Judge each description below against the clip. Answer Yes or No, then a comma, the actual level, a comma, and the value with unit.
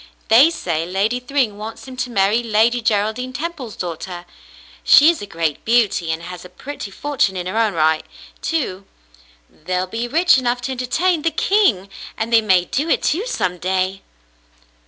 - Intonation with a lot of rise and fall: Yes, wide, 5.9 semitones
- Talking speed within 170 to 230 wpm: Yes, average, 175 wpm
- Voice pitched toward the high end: Yes, high, 220 Hz